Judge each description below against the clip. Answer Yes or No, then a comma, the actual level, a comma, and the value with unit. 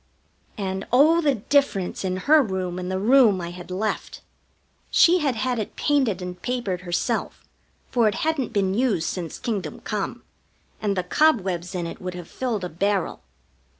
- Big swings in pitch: Yes, wide, 5.7 semitones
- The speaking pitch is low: No, high, 200 Hz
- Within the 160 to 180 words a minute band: Yes, average, 170 wpm